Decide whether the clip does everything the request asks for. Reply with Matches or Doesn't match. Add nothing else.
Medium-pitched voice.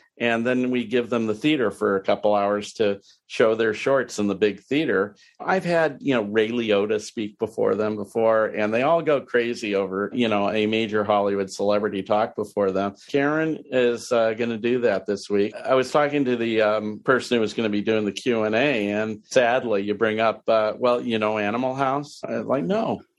Doesn't match